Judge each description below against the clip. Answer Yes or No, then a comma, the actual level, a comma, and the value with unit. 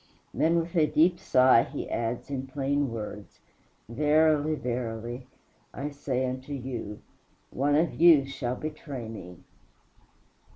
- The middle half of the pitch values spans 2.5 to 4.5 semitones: Yes, average, 3.9 semitones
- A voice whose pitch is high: No, low, 135 Hz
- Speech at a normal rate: No, slow, 125 wpm